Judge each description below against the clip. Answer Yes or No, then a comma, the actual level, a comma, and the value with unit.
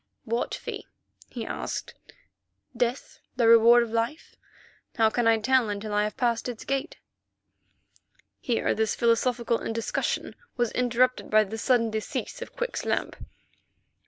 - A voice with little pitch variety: Yes, narrow, 1.8 semitones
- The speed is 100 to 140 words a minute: Yes, slow, 135 wpm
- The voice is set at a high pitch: Yes, high, 230 Hz